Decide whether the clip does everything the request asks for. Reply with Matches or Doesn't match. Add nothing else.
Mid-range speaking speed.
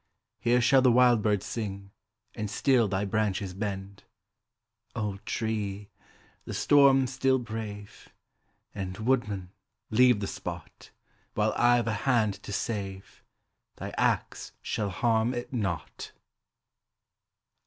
Doesn't match